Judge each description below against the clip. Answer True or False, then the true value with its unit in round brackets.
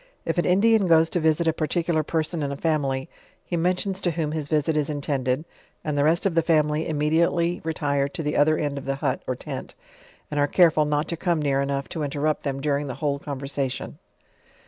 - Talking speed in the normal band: False (215 wpm)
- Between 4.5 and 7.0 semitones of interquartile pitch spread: False (2.7 semitones)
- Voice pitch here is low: False (155 Hz)